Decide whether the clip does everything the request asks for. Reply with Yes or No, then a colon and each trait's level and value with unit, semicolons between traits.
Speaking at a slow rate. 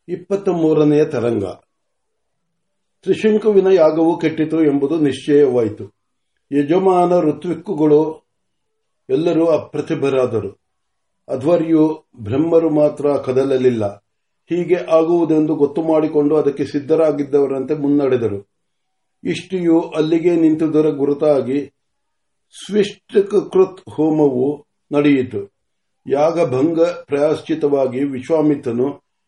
Yes: slow, 65 wpm